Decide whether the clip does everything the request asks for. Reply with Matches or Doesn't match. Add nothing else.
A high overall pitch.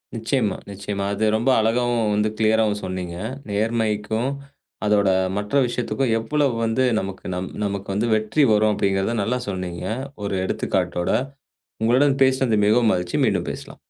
Doesn't match